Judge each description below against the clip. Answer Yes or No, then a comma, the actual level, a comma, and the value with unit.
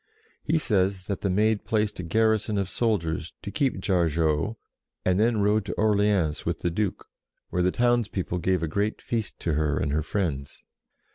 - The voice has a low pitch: Yes, low, 100 Hz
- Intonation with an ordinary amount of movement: Yes, average, 4.4 semitones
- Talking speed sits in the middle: Yes, average, 185 wpm